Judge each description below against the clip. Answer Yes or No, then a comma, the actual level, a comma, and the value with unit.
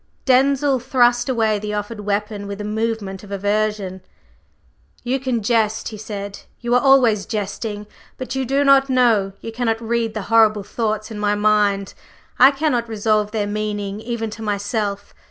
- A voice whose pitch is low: No, high, 215 Hz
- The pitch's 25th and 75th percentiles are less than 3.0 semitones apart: Yes, narrow, 2.6 semitones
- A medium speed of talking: Yes, average, 165 wpm